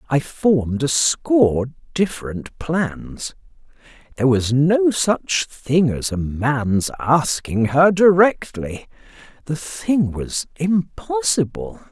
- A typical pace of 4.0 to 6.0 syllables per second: No, 3.2 syllables/s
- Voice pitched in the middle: Yes, medium, 150 Hz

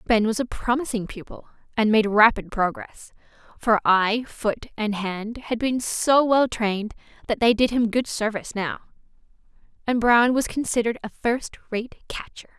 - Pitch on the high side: Yes, high, 225 Hz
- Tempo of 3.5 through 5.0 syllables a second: Yes, 4.7 syllables/s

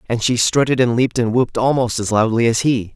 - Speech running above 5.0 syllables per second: Yes, 6.0 syllables/s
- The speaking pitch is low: Yes, low, 120 Hz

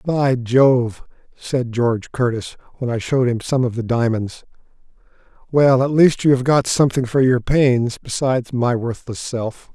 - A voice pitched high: No, low, 125 Hz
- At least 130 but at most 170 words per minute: Yes, average, 165 wpm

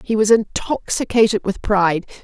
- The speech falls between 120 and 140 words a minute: Yes, slow, 135 wpm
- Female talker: Yes, female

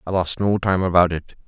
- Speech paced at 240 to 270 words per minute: Yes, fast, 245 wpm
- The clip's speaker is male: Yes, male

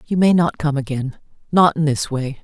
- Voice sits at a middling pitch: Yes, medium, 150 Hz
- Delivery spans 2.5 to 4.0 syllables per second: No, 5.2 syllables/s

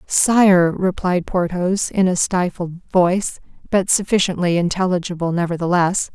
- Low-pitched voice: No, medium, 180 Hz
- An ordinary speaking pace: No, slow, 105 wpm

